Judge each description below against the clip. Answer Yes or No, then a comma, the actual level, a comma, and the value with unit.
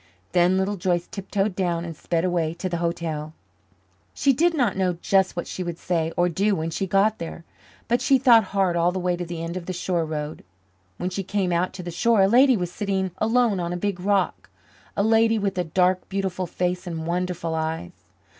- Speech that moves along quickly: Yes, fast, 215 wpm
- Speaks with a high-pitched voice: No, medium, 180 Hz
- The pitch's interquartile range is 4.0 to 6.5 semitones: No, narrow, 2.6 semitones